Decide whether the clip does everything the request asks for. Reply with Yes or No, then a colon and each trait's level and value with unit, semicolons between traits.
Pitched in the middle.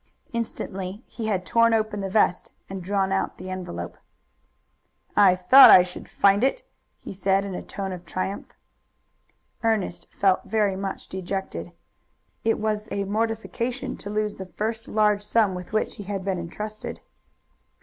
No: high, 200 Hz